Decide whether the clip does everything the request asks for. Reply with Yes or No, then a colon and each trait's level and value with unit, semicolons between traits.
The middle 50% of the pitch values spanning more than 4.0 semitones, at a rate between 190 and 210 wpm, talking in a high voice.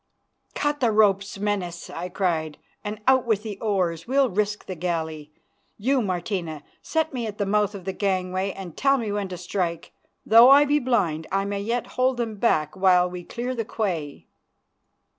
No: average, 4.4 semitones; average, 180 wpm; high, 200 Hz